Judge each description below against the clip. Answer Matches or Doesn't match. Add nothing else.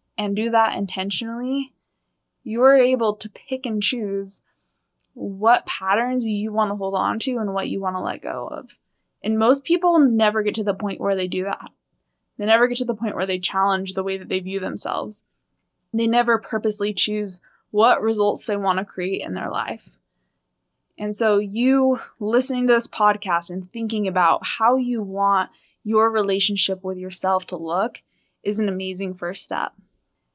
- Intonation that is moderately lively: Matches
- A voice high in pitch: Matches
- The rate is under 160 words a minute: Doesn't match